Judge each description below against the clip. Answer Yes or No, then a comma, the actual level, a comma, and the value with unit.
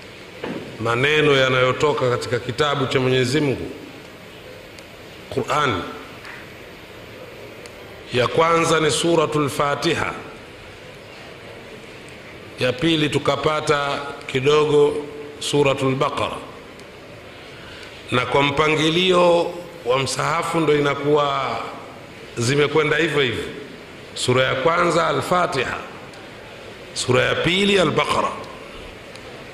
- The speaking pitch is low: No, medium, 145 Hz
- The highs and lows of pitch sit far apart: No, average, 2.8 semitones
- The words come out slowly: Yes, slow, 75 wpm